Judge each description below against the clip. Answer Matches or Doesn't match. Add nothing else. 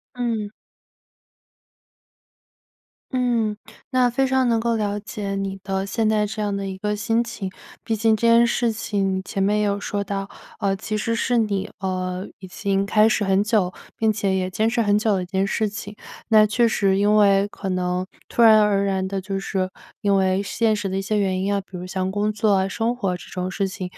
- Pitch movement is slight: Matches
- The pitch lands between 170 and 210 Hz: Matches